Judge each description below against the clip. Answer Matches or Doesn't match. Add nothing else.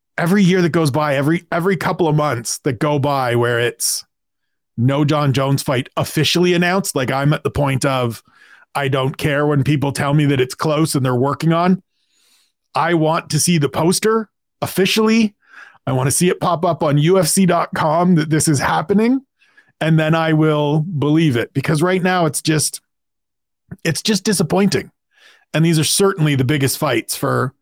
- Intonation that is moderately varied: Matches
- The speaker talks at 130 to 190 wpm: Matches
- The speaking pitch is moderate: Matches